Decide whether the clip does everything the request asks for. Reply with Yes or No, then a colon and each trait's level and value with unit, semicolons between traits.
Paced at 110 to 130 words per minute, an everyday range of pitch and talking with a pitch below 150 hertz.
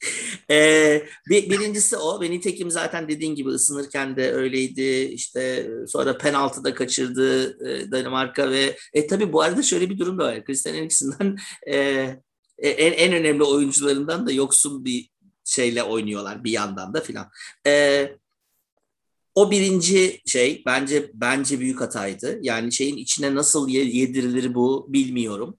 No: fast, 140 wpm; average, 4.4 semitones; medium, 140 Hz